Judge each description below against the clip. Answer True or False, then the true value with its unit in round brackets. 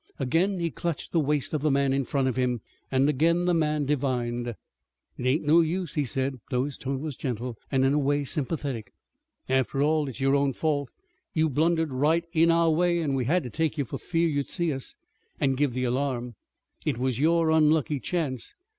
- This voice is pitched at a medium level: True (145 Hz)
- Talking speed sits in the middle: False (210 wpm)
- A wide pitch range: False (3.4 semitones)